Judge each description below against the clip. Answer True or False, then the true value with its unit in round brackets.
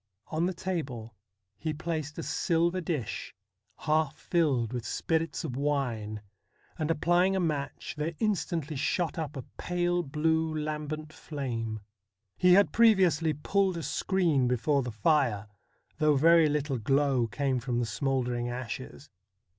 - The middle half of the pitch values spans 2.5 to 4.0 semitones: False (4.6 semitones)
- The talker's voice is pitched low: False (150 Hz)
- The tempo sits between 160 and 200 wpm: False (140 wpm)